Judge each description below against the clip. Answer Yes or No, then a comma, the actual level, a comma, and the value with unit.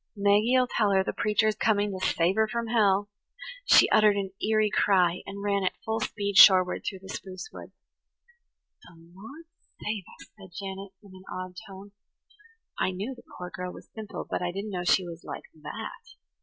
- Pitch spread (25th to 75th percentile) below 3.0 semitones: Yes, narrow, 2.4 semitones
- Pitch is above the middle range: Yes, high, 200 Hz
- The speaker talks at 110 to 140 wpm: No, average, 185 wpm